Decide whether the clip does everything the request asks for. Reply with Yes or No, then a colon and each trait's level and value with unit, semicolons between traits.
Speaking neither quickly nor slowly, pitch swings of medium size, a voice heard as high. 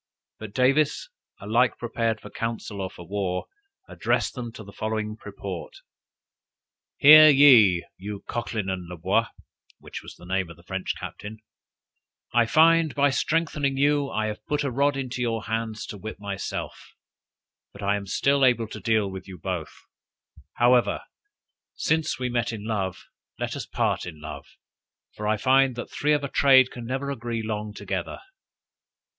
No: average, 165 wpm; average, 4.9 semitones; low, 115 Hz